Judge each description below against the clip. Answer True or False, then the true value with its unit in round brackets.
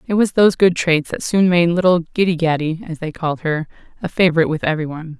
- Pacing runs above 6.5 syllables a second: True (6.7 syllables/s)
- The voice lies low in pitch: False (165 Hz)